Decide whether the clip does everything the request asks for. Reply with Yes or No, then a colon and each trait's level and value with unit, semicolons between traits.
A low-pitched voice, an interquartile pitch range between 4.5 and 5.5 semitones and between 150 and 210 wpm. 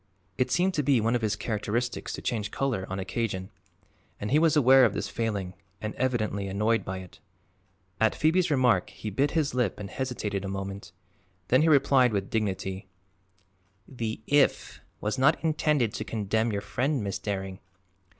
Yes: low, 110 Hz; average, 4.9 semitones; average, 170 wpm